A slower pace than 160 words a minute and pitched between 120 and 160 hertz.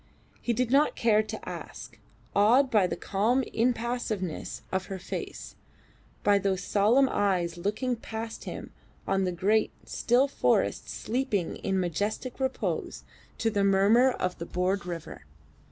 No: average, 140 wpm; high, 210 Hz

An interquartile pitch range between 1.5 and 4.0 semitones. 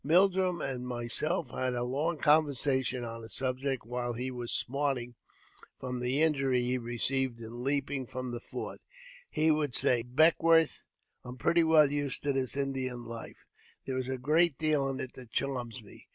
Yes: average, 2.9 semitones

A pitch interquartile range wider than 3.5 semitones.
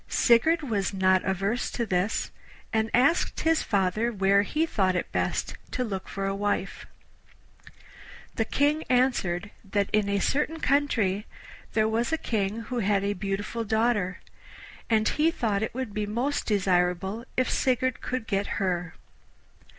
Yes: average, 4.0 semitones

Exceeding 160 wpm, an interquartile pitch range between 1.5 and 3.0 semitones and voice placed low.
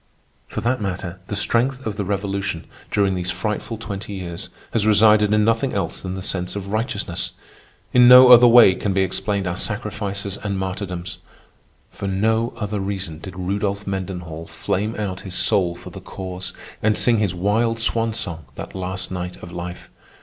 Yes: average, 175 wpm; narrow, 2.6 semitones; low, 100 Hz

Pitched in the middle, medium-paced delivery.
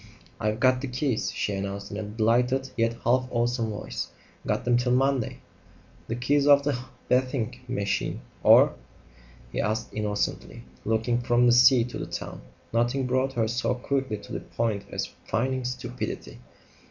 No: low, 120 Hz; average, 165 wpm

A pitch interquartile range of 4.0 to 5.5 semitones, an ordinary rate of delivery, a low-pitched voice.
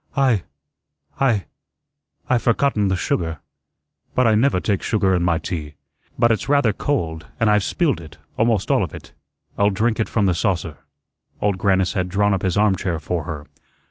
Yes: average, 4.3 semitones; average, 175 wpm; low, 100 Hz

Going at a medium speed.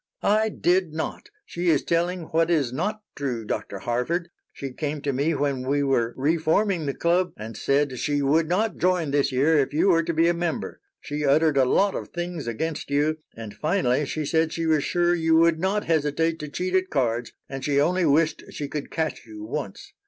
No: fast, 210 wpm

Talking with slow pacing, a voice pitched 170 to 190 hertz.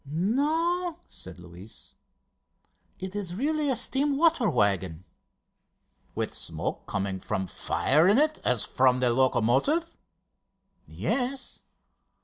Yes: slow, 110 wpm; medium, 185 Hz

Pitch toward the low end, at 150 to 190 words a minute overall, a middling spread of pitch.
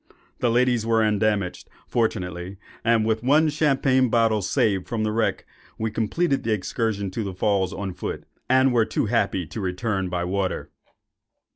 Yes: low, 110 Hz; average, 160 wpm; average, 3.3 semitones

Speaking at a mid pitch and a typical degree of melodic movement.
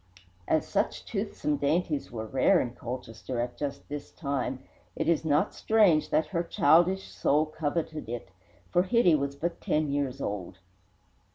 Yes: medium, 145 Hz; average, 4.2 semitones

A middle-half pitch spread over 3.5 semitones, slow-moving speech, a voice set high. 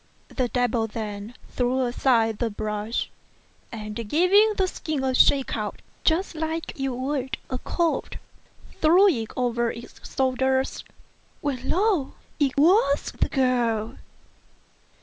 Yes: average, 4.7 semitones; slow, 125 wpm; very high, 260 Hz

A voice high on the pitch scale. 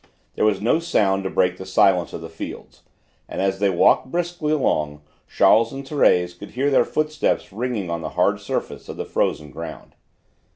No: very low, 95 Hz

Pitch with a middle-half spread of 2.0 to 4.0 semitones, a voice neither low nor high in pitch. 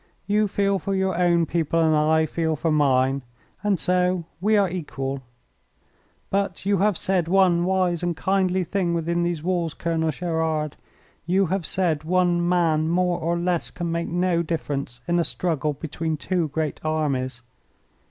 Yes: narrow, 2.6 semitones; medium, 170 Hz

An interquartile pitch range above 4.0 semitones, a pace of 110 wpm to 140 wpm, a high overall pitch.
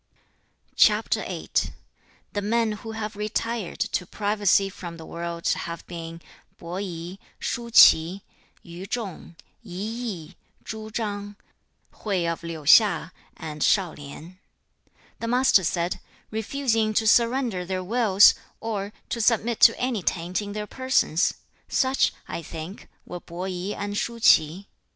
Yes: average, 4.4 semitones; slow, 135 wpm; high, 200 Hz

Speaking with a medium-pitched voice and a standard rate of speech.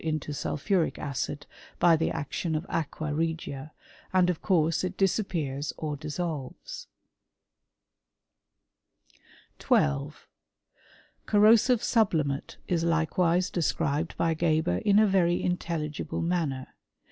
No: medium, 165 Hz; slow, 105 wpm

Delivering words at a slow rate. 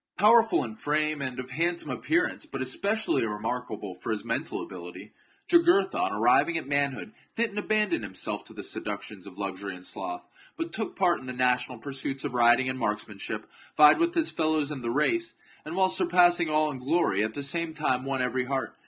No: average, 195 wpm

